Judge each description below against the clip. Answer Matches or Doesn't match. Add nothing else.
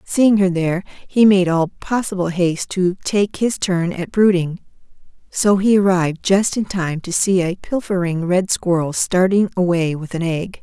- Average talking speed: Matches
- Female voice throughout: Matches